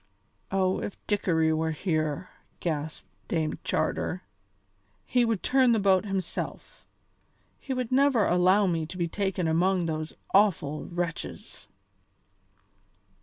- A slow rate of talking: Yes, slow, 120 wpm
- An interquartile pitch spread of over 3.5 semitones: Yes, average, 4.0 semitones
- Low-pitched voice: No, medium, 185 Hz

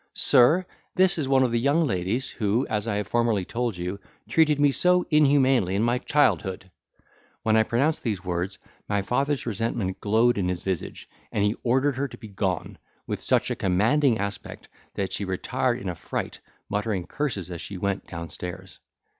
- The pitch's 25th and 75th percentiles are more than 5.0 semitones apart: Yes, wide, 5.6 semitones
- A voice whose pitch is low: Yes, low, 110 Hz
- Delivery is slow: No, average, 180 wpm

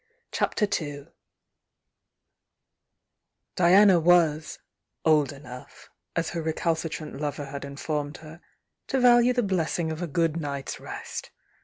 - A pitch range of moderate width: Yes, average, 3.2 semitones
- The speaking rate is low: Yes, slow, 115 wpm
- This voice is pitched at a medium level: Yes, medium, 160 Hz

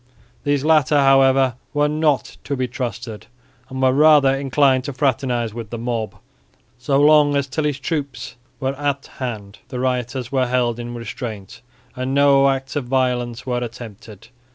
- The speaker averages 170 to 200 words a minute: No, average, 155 wpm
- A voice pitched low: Yes, low, 130 Hz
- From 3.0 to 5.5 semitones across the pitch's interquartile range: No, narrow, 2.6 semitones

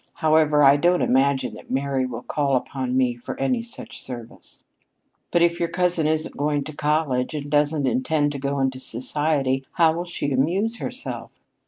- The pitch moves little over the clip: No, average, 3.1 semitones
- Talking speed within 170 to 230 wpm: Yes, average, 175 wpm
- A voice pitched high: No, medium, 145 Hz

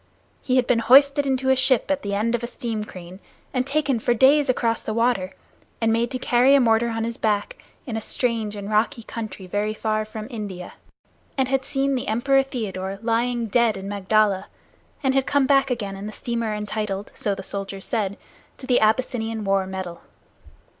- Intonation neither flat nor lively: Yes, average, 3.6 semitones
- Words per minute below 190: No, average, 195 wpm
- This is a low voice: No, high, 225 Hz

